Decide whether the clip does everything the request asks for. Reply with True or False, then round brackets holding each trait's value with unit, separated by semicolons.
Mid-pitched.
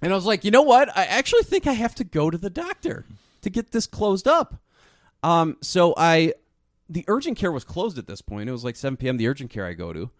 True (170 Hz)